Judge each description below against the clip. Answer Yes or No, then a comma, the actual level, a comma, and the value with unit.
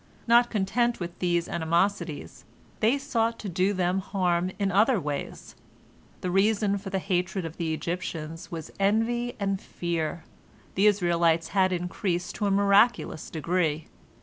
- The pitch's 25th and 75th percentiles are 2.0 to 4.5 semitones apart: Yes, average, 3.1 semitones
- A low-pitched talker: No, medium, 185 Hz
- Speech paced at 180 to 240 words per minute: No, average, 145 wpm